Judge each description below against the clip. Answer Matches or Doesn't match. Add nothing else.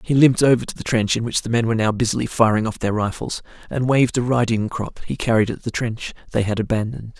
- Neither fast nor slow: Doesn't match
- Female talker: Doesn't match